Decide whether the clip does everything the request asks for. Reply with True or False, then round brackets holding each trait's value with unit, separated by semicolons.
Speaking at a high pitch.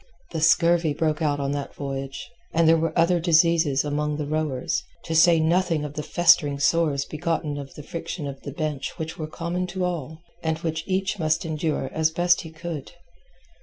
False (160 Hz)